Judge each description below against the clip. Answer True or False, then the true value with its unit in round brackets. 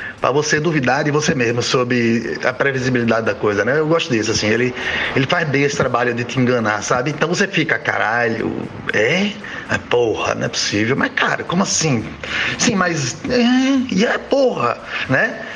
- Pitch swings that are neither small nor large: False (7.4 semitones)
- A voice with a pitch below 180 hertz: True (140 Hz)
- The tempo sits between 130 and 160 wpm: False (180 wpm)